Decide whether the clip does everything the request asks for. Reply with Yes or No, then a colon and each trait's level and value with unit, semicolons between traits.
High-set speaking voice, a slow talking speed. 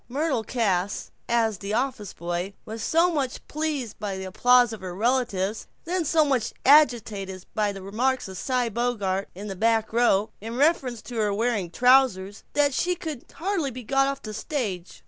No: high, 230 Hz; average, 180 wpm